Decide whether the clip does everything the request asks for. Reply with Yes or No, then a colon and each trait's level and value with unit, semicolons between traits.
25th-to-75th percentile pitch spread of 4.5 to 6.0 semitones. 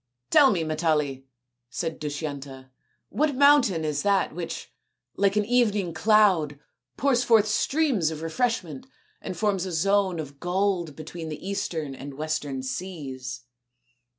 Yes: wide, 5.5 semitones